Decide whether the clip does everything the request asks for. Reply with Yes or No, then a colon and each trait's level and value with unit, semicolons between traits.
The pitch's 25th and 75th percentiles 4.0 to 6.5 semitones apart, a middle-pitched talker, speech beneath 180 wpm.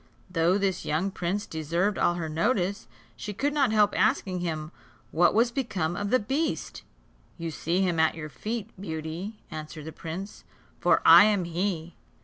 Yes: average, 4.3 semitones; medium, 180 Hz; average, 165 wpm